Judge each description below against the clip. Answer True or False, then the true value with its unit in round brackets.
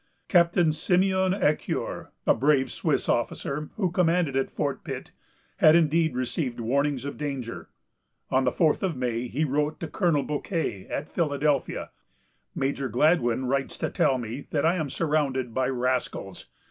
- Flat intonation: False (4.1 semitones)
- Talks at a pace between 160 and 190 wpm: False (150 wpm)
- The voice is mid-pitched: True (145 Hz)